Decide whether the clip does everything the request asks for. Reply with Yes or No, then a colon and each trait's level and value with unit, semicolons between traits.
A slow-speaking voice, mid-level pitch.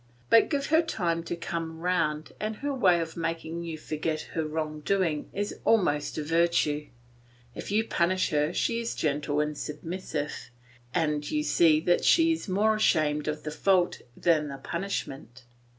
No: average, 165 wpm; medium, 165 Hz